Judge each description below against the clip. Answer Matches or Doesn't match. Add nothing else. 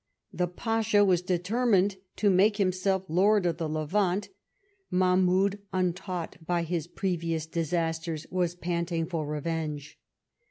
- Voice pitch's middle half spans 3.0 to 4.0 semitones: Doesn't match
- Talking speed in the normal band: Doesn't match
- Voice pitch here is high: Doesn't match